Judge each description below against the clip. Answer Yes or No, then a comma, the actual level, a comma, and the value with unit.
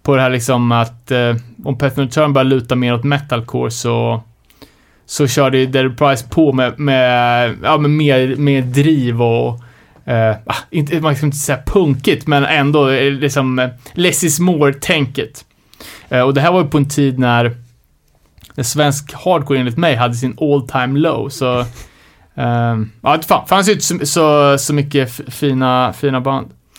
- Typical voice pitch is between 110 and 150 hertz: Yes, low, 135 Hz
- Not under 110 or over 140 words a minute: No, average, 170 wpm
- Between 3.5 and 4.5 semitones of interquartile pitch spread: No, average, 2.9 semitones